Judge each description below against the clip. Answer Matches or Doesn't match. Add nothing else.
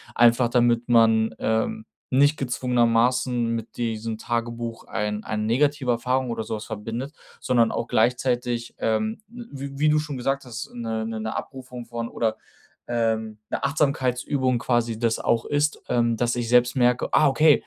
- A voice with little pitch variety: Matches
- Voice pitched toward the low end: Matches